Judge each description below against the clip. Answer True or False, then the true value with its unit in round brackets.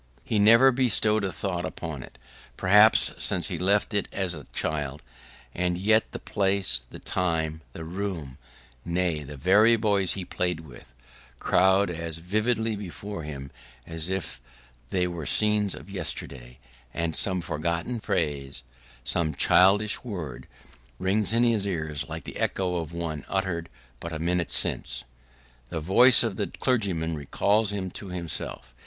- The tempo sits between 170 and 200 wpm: False (150 wpm)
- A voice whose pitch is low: True (90 Hz)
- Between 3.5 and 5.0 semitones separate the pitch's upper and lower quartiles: True (4.2 semitones)